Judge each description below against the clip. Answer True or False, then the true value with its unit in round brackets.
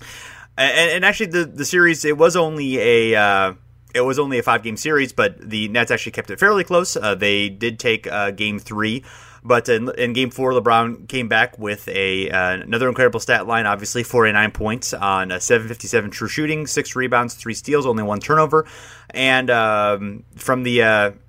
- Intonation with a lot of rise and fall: False (4.0 semitones)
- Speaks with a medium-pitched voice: False (120 Hz)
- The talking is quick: False (195 wpm)